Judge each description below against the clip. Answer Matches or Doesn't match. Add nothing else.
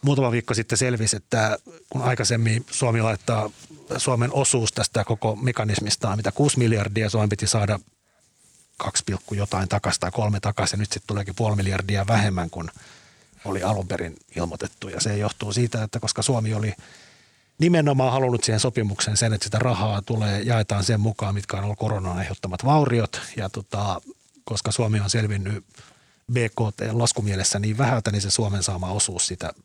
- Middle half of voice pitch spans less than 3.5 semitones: Matches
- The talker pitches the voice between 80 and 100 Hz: Doesn't match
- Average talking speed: Doesn't match